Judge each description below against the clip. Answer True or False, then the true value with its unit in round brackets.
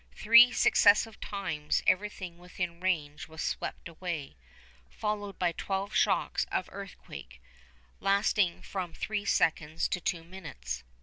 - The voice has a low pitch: False (180 Hz)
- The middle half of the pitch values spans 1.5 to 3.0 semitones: False (3.7 semitones)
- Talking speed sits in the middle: False (120 wpm)